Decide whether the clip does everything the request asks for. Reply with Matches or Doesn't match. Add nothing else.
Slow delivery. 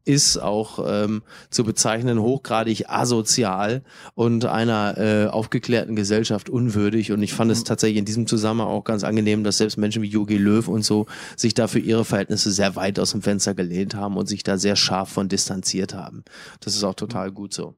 Doesn't match